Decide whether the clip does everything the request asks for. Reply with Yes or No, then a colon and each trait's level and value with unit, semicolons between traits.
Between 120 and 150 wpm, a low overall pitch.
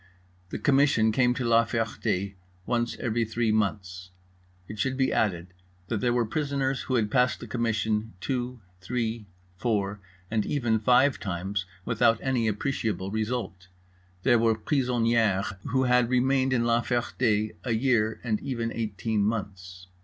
Yes: average, 145 wpm; low, 115 Hz